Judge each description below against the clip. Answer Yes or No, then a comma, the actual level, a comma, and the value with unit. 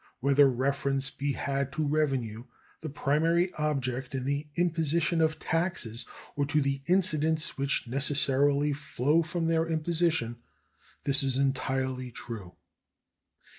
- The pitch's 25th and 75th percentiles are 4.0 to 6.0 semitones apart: No, average, 3.1 semitones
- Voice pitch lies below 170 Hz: Yes, medium, 140 Hz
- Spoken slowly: Yes, slow, 125 wpm